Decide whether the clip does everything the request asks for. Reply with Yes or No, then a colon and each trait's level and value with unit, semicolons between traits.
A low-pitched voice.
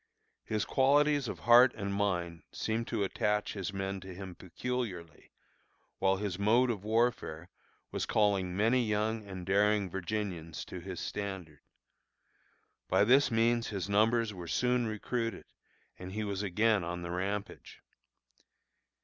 Yes: low, 105 Hz